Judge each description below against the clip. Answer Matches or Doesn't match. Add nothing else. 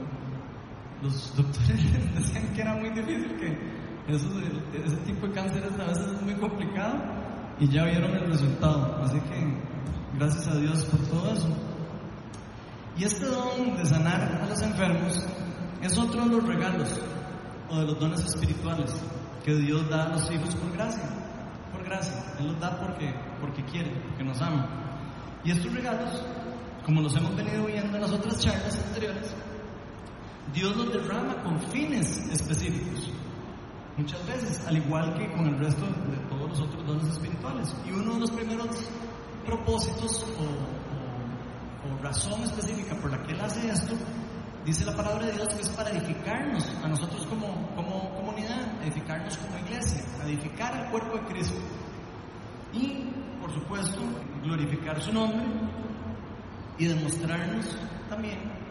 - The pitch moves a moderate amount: Doesn't match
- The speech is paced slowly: Doesn't match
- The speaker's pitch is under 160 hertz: Doesn't match